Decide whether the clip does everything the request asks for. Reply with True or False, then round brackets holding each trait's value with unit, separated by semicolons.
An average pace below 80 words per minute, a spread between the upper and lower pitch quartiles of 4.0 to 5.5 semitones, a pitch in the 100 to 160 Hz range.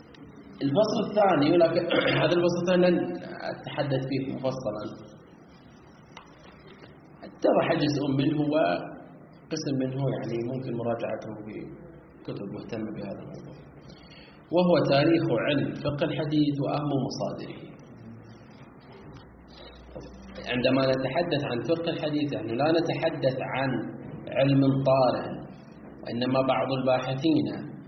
False (95 wpm; 4.4 semitones; 135 Hz)